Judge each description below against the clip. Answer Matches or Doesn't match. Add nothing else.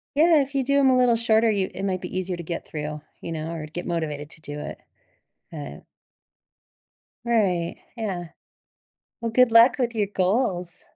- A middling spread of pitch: Doesn't match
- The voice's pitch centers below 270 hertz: Matches